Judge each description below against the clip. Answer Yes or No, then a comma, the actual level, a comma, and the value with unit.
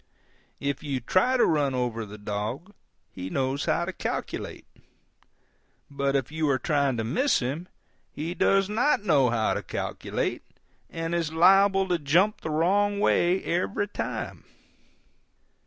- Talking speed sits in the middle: Yes, average, 145 wpm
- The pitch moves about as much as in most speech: No, wide, 6.2 semitones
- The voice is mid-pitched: Yes, medium, 155 Hz